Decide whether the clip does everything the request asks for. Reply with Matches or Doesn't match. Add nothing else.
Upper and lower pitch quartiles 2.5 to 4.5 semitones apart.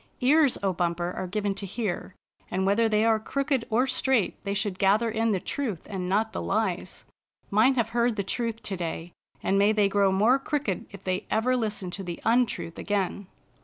Matches